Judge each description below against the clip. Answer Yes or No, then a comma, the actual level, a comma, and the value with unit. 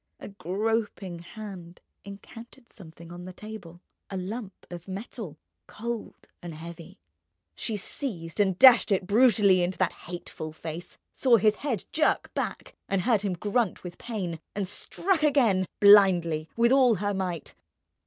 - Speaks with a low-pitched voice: No, high, 195 Hz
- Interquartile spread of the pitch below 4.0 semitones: No, average, 4.3 semitones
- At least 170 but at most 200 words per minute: No, average, 145 wpm